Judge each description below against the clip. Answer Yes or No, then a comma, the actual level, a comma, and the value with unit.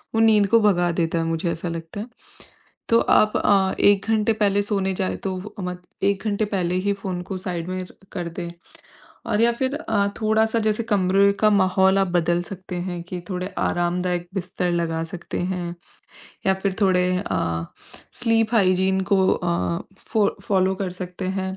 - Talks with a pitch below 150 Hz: No, high, 190 Hz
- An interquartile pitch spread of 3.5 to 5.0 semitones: No, narrow, 2.5 semitones